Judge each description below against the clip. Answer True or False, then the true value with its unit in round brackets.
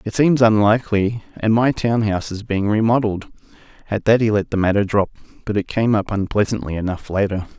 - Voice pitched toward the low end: True (105 Hz)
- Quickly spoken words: False (190 wpm)